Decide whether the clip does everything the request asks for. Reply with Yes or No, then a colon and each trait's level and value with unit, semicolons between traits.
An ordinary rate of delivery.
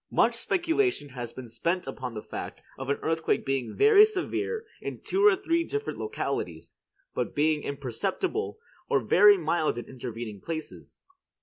Yes: average, 150 wpm